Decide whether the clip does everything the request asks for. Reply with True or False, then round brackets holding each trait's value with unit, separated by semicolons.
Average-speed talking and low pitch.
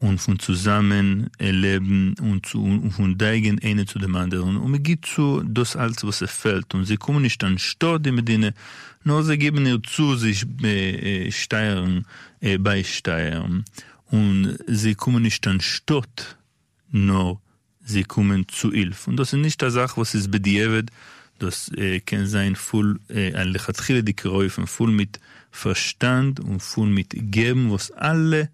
False (165 wpm; 105 Hz)